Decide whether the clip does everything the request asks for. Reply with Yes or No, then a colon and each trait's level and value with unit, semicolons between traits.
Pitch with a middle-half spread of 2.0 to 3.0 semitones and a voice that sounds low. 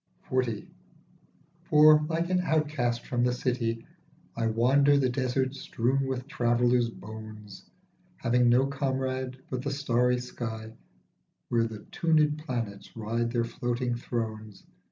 Yes: average, 2.7 semitones; low, 125 Hz